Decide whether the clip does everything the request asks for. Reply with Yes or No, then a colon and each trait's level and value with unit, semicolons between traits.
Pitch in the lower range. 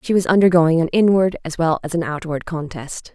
No: medium, 165 Hz